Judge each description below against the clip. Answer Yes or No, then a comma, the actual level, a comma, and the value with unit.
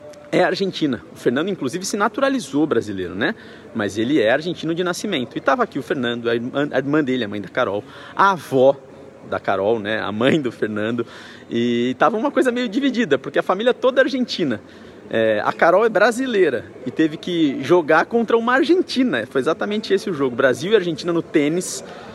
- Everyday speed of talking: No, fast, 190 wpm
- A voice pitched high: No, medium, 170 Hz